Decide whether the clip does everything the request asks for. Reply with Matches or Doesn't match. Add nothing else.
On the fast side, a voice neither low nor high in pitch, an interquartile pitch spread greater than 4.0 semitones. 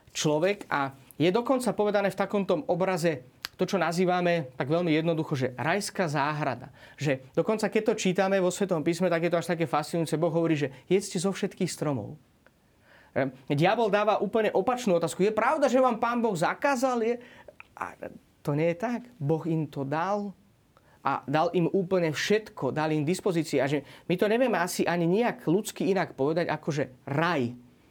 Matches